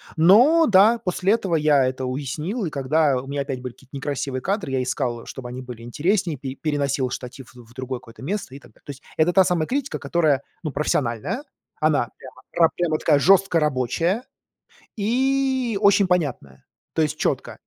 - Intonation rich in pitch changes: Yes, wide, 6.4 semitones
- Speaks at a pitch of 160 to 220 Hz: No, medium, 150 Hz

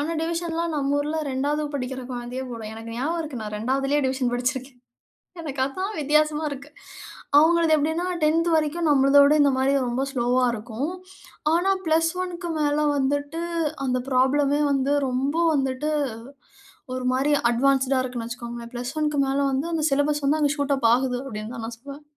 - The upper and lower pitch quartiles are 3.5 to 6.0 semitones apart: No, average, 3.0 semitones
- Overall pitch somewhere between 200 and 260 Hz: No, very high, 275 Hz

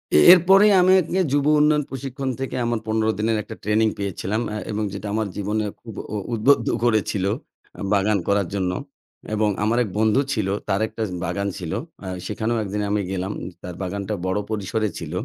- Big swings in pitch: No, average, 2.8 semitones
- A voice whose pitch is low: Yes, low, 110 Hz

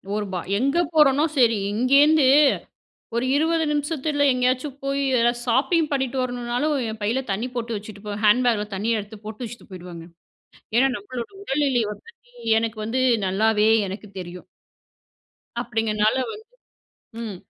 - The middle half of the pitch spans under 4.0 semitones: No, average, 4.6 semitones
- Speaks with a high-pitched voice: Yes, high, 240 Hz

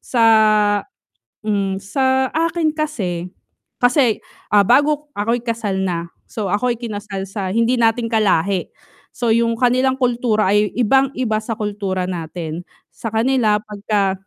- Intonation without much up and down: No, average, 4.1 semitones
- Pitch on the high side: Yes, high, 220 Hz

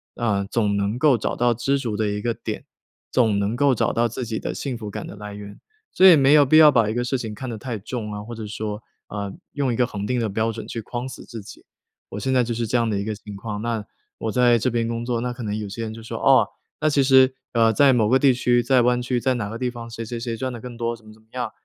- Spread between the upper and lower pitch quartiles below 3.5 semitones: Yes, narrow, 2.6 semitones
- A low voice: Yes, low, 115 Hz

